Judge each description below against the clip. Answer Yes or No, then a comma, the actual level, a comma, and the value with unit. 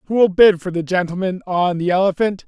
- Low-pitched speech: No, medium, 185 Hz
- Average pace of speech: Yes, average, 195 wpm